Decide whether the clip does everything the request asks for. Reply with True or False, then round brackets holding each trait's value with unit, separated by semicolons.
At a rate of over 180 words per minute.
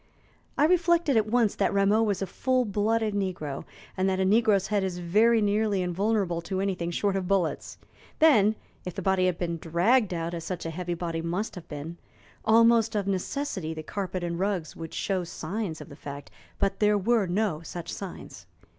True (190 wpm)